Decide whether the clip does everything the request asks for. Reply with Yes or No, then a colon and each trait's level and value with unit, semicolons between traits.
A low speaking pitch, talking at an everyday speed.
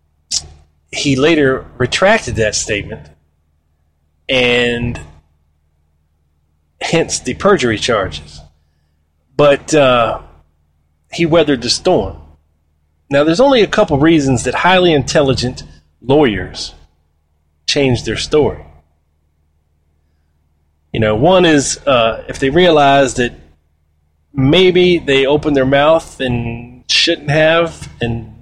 No: very low, 80 Hz; slow, 100 wpm